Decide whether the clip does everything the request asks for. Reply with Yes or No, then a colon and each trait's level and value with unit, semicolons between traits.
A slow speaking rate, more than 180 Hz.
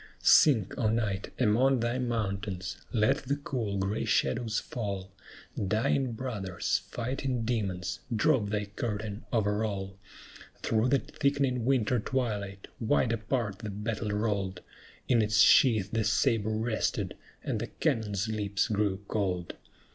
No: slow, 130 wpm; low, 110 Hz